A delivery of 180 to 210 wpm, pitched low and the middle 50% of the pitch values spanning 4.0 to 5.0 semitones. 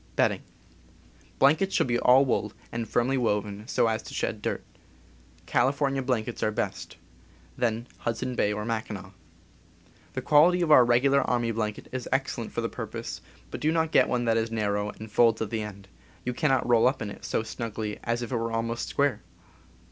No: average, 195 wpm; low, 115 Hz; average, 3.1 semitones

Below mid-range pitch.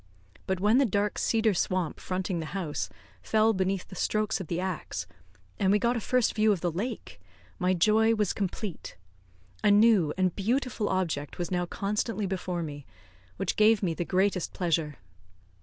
No: high, 190 Hz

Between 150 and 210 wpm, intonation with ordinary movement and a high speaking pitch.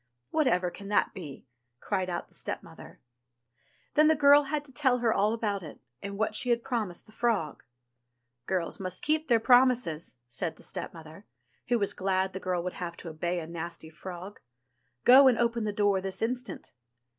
No: average, 190 wpm; wide, 5.7 semitones; high, 200 Hz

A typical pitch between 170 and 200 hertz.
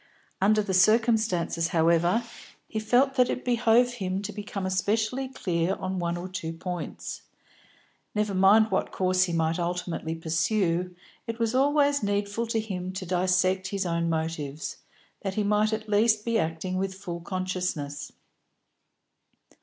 Yes: high, 190 Hz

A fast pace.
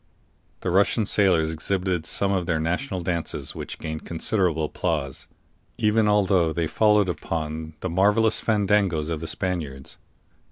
No: slow, 135 wpm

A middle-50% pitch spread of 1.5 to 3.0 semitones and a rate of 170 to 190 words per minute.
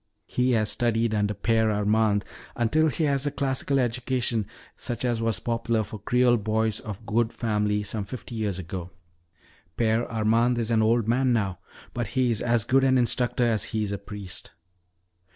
Yes: narrow, 2.4 semitones; average, 175 wpm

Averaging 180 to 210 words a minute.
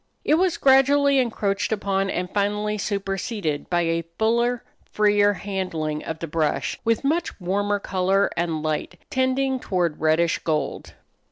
No: average, 140 wpm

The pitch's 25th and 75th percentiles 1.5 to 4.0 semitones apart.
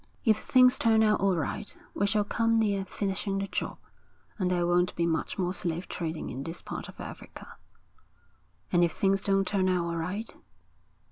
Yes: average, 3.0 semitones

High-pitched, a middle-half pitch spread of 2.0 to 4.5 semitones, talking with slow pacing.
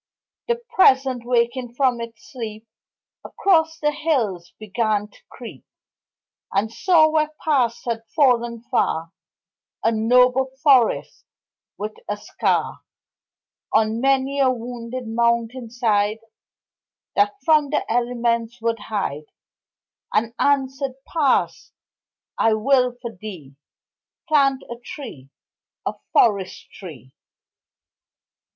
Yes: high, 235 Hz; average, 3.5 semitones; slow, 105 wpm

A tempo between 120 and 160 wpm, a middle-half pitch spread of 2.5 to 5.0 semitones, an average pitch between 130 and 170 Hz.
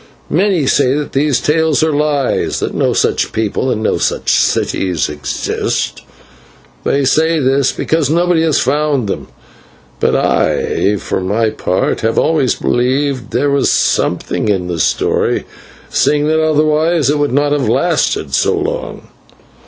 Yes: average, 150 wpm; average, 4.0 semitones; medium, 140 Hz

